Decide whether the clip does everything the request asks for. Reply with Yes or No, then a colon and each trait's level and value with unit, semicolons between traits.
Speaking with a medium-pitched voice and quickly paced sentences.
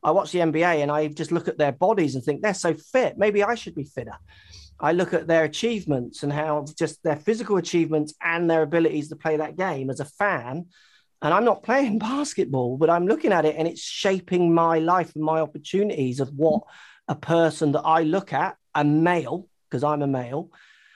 Yes: medium, 160 Hz; fast, 210 wpm